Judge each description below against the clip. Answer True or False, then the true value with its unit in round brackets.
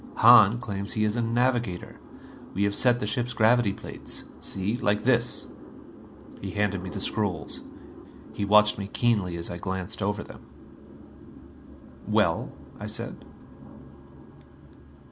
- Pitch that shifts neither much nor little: True (3.0 semitones)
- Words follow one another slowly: True (130 wpm)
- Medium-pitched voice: False (105 Hz)